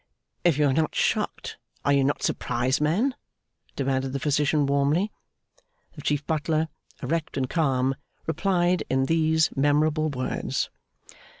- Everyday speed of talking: No, slow, 130 wpm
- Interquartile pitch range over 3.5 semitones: No, average, 2.8 semitones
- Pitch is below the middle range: No, medium, 150 Hz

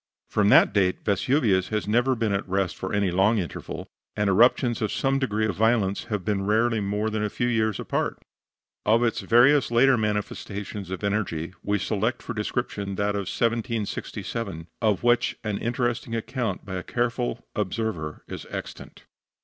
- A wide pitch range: No, average, 3.0 semitones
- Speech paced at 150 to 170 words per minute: Yes, average, 165 wpm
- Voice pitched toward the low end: Yes, low, 105 Hz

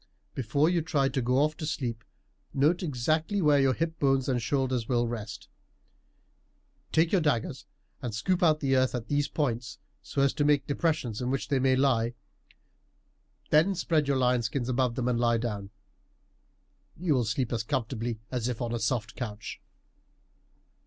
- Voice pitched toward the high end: No, low, 130 Hz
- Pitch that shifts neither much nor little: Yes, average, 3.8 semitones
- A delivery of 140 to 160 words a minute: No, average, 175 wpm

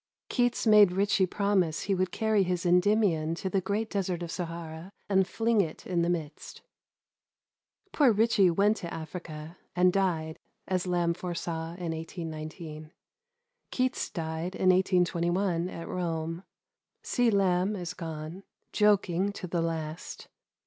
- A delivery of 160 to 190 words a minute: No, slow, 135 wpm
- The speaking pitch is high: No, medium, 180 Hz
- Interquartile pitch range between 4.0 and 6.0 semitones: No, average, 3.0 semitones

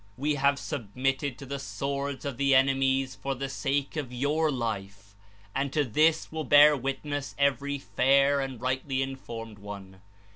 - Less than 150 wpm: No, average, 155 wpm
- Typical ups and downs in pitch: No, narrow, 1.8 semitones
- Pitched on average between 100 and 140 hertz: Yes, low, 135 Hz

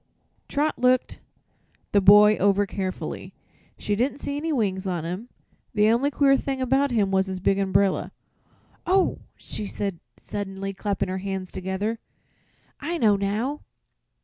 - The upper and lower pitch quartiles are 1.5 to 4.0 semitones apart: No, average, 4.9 semitones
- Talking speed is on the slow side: No, average, 150 wpm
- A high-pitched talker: Yes, high, 205 Hz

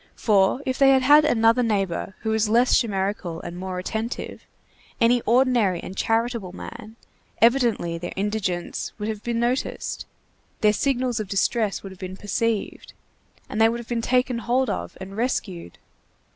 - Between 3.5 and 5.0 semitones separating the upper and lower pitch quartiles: Yes, average, 3.8 semitones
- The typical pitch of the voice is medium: No, high, 225 Hz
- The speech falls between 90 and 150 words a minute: No, average, 160 wpm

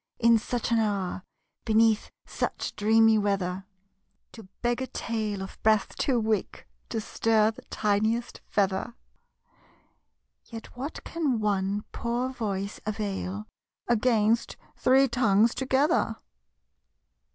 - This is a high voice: Yes, high, 220 Hz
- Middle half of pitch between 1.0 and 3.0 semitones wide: Yes, narrow, 2.6 semitones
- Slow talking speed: Yes, slow, 110 wpm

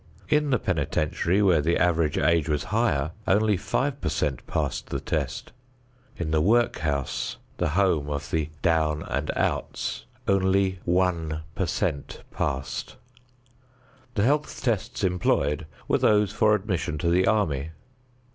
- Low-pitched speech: Yes, very low, 85 Hz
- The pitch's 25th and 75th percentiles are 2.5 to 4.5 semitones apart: No, average, 5.1 semitones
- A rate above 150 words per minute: No, average, 140 wpm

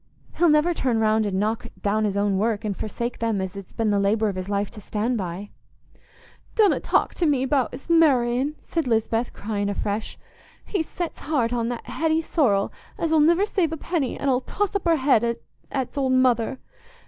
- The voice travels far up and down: Yes, wide, 6.3 semitones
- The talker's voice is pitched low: No, high, 240 Hz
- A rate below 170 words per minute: No, average, 195 wpm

